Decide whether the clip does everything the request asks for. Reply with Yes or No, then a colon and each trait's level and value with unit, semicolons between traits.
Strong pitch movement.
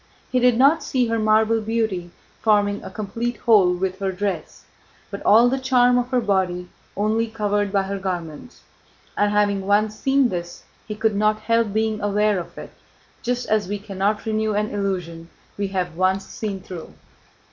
No: narrow, 2.6 semitones